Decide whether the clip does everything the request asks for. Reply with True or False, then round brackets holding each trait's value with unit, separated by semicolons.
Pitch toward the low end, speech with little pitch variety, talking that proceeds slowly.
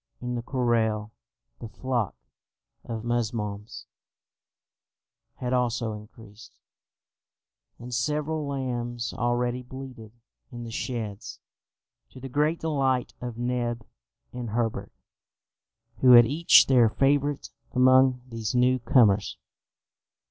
True (120 Hz; 2.1 semitones; 105 wpm)